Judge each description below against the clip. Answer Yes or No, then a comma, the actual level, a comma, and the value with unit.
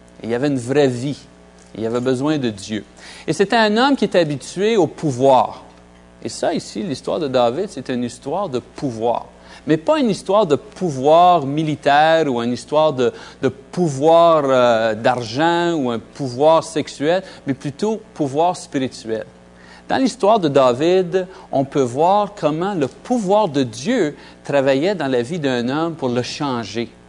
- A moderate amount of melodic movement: No, wide, 5.9 semitones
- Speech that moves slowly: No, average, 170 wpm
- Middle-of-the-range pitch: Yes, medium, 145 Hz